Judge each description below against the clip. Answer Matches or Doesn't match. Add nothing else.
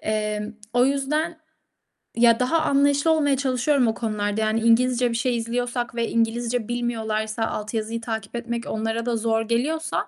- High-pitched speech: Matches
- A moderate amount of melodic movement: Doesn't match